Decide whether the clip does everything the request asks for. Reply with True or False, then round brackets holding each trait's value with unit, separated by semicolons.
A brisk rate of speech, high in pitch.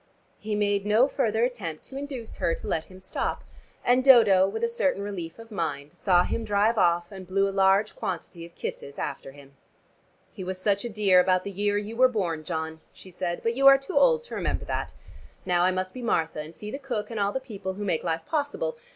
True (230 wpm; 200 Hz)